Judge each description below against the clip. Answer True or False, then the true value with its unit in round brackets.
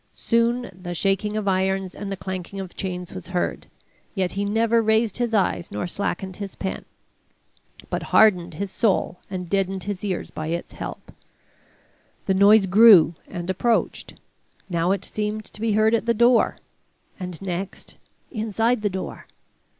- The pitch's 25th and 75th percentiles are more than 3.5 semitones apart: False (2.8 semitones)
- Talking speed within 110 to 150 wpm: False (160 wpm)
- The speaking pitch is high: True (195 Hz)